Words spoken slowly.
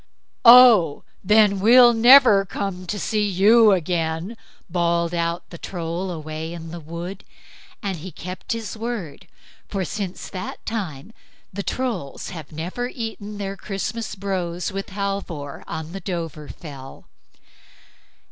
Yes: slow, 130 wpm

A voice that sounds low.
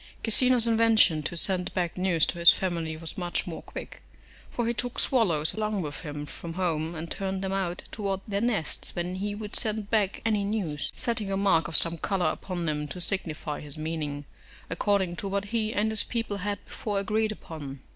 No: high, 190 Hz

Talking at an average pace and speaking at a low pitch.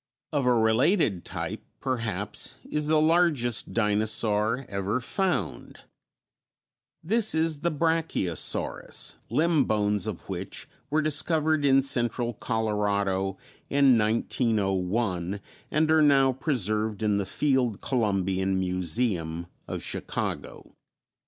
No: slow, 105 wpm; low, 115 Hz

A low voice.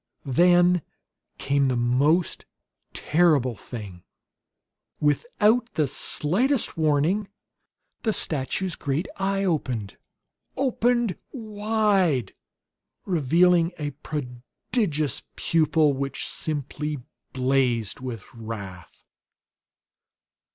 No: medium, 155 Hz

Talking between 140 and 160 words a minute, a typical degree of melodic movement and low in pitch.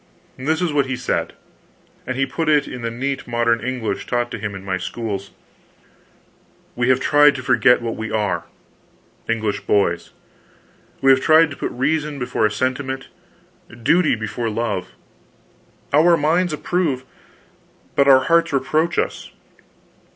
Yes: average, 145 wpm; average, 4.2 semitones; low, 130 Hz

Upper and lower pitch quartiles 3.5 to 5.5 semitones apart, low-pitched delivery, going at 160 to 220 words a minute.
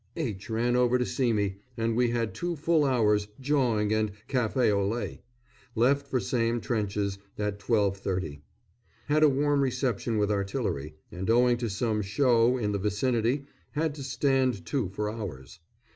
Yes: average, 3.9 semitones; low, 115 Hz; average, 165 wpm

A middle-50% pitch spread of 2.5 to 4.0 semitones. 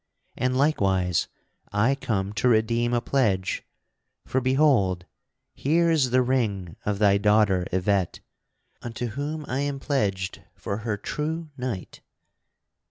No: average, 5.3 semitones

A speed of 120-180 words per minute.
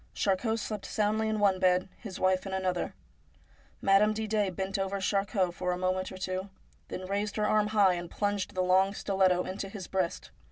No: average, 195 wpm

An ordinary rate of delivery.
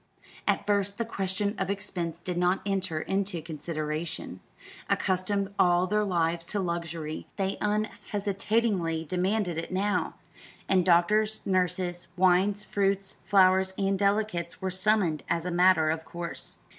No: slow, 130 wpm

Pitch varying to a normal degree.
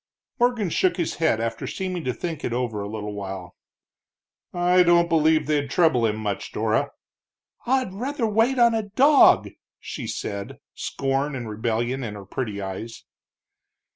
No: wide, 9.0 semitones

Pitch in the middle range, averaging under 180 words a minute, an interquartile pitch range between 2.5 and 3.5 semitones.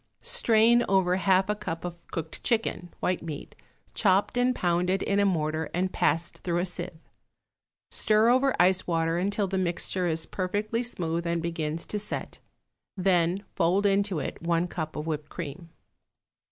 Yes: medium, 180 Hz; average, 160 wpm; average, 3.1 semitones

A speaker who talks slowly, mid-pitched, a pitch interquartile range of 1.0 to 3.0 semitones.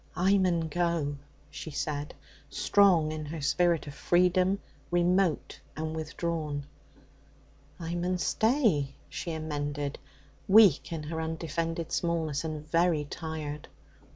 Yes: slow, 115 wpm; medium, 160 Hz; narrow, 2.6 semitones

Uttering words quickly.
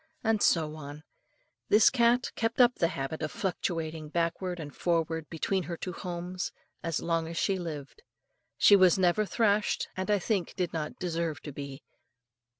No: average, 165 wpm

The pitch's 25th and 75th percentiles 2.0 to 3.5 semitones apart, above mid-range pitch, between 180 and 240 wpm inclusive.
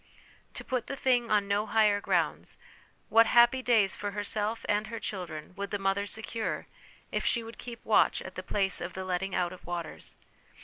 Yes: average, 2.9 semitones; high, 205 Hz; average, 190 wpm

